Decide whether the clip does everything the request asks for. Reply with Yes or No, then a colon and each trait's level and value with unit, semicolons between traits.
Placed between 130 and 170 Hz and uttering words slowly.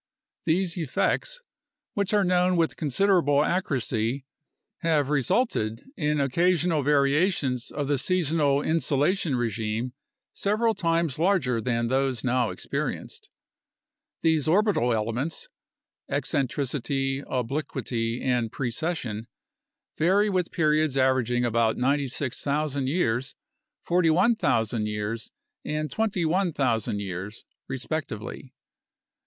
Yes: medium, 140 Hz; slow, 90 wpm